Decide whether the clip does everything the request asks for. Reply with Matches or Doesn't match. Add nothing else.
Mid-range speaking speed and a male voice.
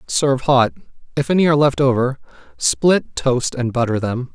Matches